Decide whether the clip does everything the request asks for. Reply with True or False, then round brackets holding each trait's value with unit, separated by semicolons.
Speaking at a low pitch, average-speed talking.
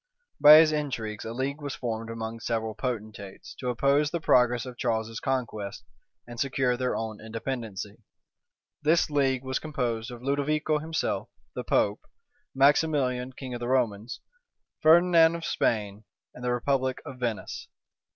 True (125 Hz; 145 wpm)